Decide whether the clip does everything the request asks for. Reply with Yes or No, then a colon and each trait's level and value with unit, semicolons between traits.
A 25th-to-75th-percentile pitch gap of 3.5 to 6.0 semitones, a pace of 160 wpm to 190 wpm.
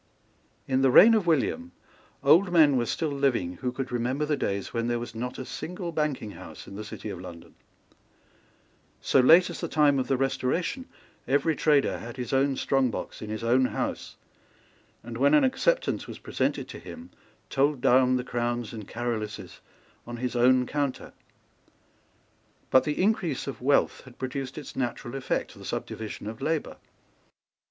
Yes: average, 3.8 semitones; average, 170 wpm